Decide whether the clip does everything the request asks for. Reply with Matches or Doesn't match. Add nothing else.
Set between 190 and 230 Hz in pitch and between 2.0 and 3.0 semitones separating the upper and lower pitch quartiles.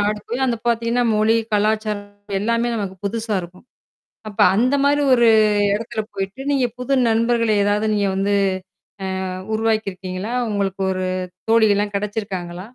Matches